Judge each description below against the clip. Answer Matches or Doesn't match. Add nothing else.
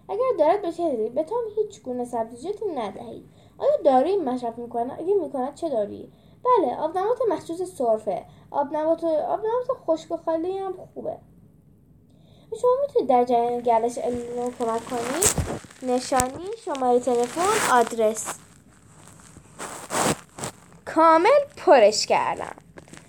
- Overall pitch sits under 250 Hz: Doesn't match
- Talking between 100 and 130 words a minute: Matches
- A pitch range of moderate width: Doesn't match